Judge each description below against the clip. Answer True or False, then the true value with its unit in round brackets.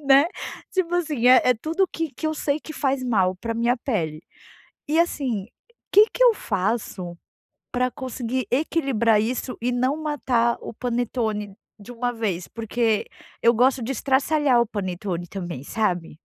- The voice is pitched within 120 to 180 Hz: False (245 Hz)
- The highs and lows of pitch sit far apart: False (4.5 semitones)